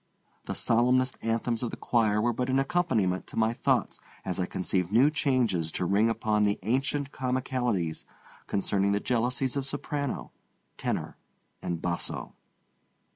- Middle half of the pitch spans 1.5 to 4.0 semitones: No, average, 4.4 semitones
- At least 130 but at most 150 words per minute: Yes, average, 145 wpm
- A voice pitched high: No, low, 115 Hz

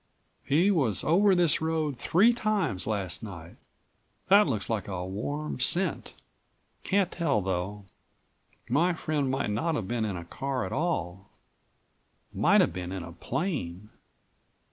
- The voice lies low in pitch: Yes, low, 130 Hz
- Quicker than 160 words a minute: No, average, 145 wpm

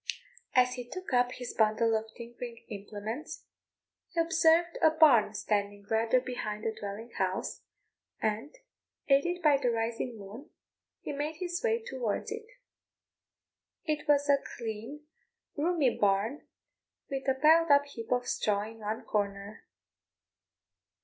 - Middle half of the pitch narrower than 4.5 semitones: No, wide, 5.6 semitones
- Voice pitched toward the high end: Yes, high, 245 Hz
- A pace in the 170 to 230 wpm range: No, slow, 135 wpm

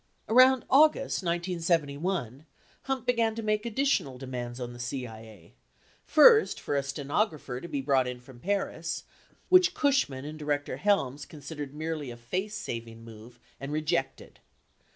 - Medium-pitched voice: Yes, medium, 150 Hz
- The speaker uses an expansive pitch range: Yes, wide, 8.5 semitones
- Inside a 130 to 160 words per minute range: Yes, average, 145 wpm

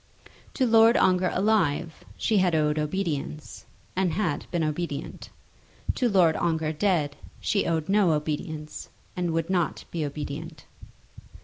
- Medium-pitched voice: Yes, medium, 165 Hz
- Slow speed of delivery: Yes, slow, 130 wpm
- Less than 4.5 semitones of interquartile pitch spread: Yes, average, 3.6 semitones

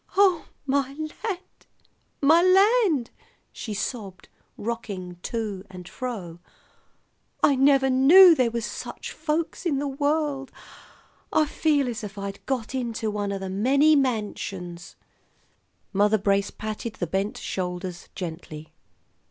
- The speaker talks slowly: Yes, slow, 125 wpm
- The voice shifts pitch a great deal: Yes, wide, 6.5 semitones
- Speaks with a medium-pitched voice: No, high, 235 Hz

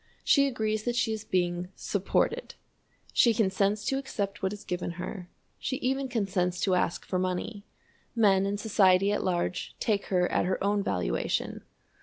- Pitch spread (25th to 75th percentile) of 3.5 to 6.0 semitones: No, average, 3.1 semitones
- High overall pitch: Yes, high, 200 Hz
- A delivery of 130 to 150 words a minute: No, average, 165 wpm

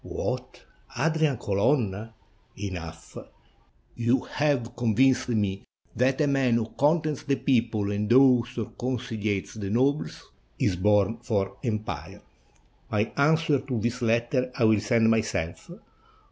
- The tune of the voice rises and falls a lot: No, average, 3.9 semitones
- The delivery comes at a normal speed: No, slow, 130 wpm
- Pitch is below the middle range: Yes, low, 115 Hz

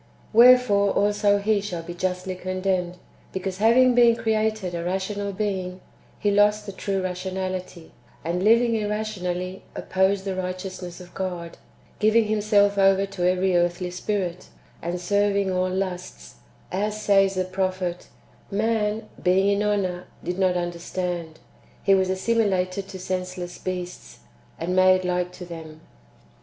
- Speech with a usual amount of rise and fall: No, narrow, 2.1 semitones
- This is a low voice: No, high, 190 Hz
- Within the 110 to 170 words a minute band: Yes, average, 145 wpm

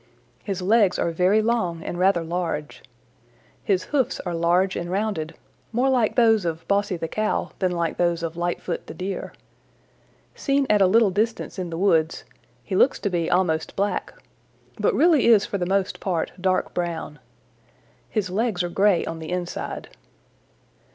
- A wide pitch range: No, average, 3.5 semitones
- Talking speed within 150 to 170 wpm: Yes, average, 165 wpm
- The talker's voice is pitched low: No, medium, 185 Hz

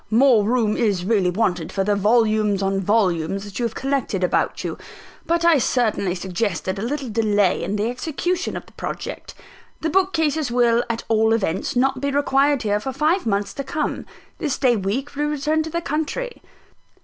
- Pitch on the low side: No, high, 230 Hz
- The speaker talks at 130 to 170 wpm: No, average, 185 wpm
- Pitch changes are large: Yes, wide, 5.8 semitones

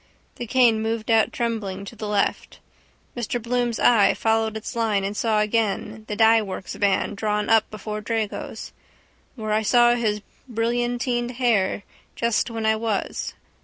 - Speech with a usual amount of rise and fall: No, narrow, 1.8 semitones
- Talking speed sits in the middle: Yes, average, 150 wpm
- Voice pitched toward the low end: No, high, 220 Hz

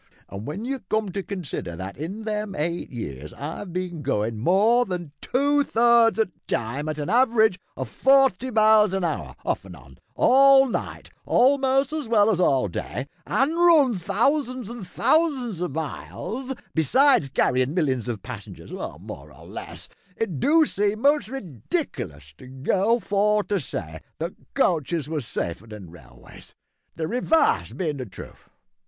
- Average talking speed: Yes, average, 160 wpm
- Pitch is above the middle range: Yes, high, 195 Hz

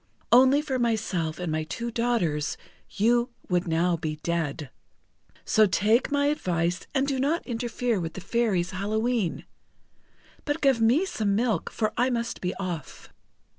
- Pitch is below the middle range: No, high, 220 Hz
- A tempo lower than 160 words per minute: Yes, average, 150 wpm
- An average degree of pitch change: No, wide, 5.8 semitones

